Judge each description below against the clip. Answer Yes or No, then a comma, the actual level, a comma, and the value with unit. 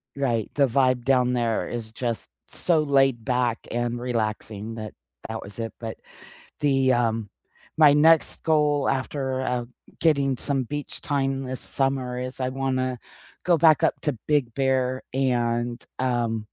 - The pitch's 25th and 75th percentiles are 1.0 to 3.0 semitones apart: Yes, narrow, 2.5 semitones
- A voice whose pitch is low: Yes, low, 130 Hz